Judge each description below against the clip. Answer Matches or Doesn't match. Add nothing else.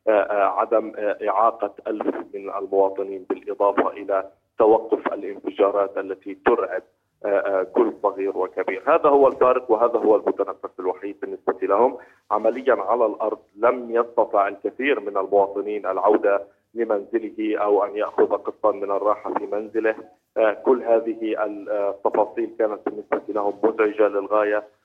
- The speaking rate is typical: Matches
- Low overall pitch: Matches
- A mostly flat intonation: Matches